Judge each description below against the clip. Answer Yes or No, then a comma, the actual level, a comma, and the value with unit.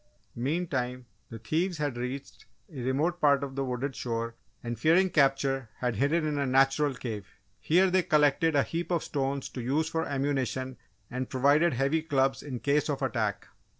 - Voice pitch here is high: No, medium, 140 Hz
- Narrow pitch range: No, average, 3.2 semitones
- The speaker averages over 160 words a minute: Yes, average, 175 wpm